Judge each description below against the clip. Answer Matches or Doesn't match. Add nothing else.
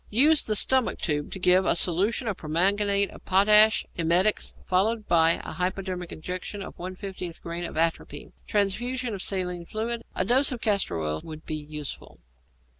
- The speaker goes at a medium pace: Matches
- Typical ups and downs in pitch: Matches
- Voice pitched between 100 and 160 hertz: Doesn't match